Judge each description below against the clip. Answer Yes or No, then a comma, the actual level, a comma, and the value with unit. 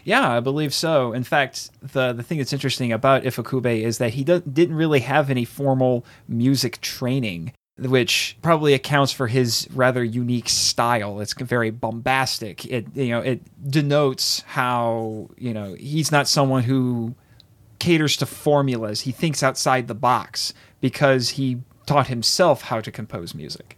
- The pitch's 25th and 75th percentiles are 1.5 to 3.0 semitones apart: Yes, average, 2.7 semitones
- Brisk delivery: No, average, 160 wpm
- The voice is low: Yes, low, 130 Hz